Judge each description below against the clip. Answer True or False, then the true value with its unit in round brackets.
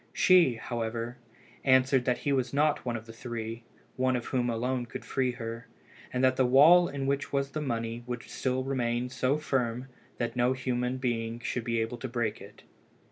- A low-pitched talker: True (125 Hz)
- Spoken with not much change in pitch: True (1.9 semitones)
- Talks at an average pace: True (190 wpm)